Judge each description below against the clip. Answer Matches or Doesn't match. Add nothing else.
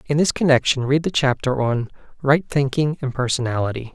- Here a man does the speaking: Matches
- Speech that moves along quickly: Doesn't match